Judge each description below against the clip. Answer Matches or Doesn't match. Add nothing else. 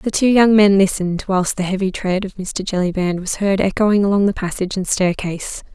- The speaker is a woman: Matches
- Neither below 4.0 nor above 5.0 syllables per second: Doesn't match